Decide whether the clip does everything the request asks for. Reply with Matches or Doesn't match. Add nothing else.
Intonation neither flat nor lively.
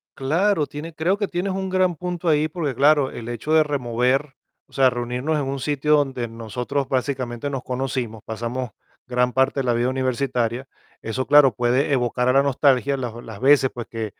Matches